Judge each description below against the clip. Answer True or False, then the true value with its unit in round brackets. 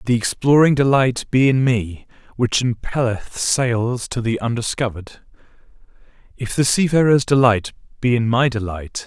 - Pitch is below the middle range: True (120 Hz)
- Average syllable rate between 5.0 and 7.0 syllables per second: False (4.7 syllables/s)